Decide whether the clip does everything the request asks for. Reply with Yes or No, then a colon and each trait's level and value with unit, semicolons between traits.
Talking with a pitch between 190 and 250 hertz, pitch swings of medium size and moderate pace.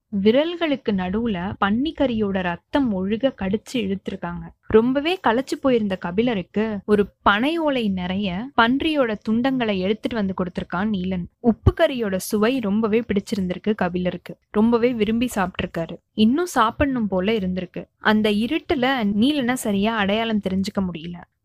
Yes: high, 215 Hz; average, 4.4 semitones; average, 115 wpm